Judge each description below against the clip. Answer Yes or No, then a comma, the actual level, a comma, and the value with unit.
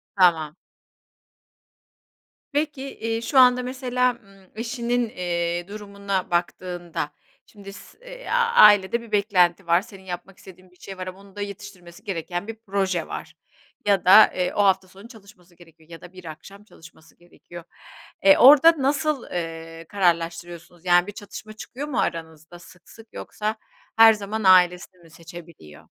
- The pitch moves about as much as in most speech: Yes, average, 3.9 semitones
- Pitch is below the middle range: No, high, 190 Hz